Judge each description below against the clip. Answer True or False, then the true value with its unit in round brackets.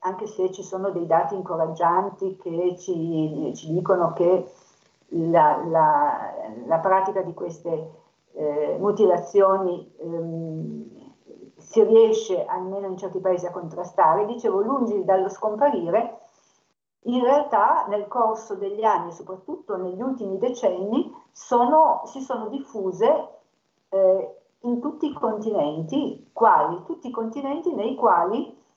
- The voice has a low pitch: False (195 Hz)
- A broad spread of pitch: True (5.7 semitones)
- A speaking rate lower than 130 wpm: True (120 wpm)